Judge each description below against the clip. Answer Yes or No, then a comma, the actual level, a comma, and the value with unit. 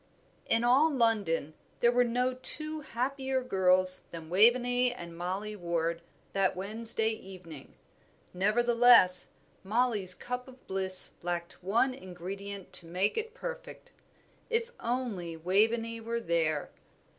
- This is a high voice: Yes, high, 215 Hz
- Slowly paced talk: Yes, slow, 120 wpm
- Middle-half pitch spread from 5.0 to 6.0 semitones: Yes, average, 5.3 semitones